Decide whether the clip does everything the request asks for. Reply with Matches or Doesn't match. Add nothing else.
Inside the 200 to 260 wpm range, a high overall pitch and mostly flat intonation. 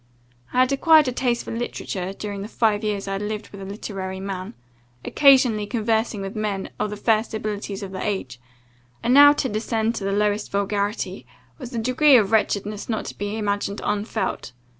Doesn't match